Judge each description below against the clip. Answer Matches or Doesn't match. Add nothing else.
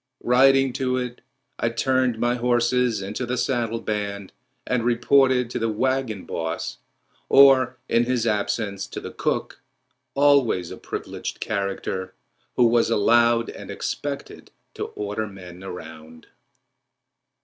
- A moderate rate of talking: Doesn't match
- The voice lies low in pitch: Matches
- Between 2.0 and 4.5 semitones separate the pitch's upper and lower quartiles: Matches